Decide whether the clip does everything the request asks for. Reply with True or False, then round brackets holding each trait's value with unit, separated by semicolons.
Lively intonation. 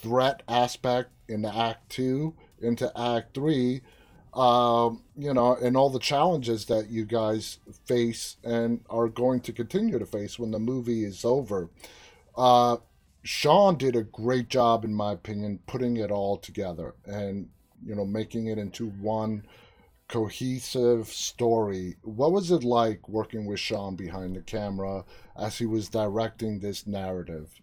False (3.0 semitones)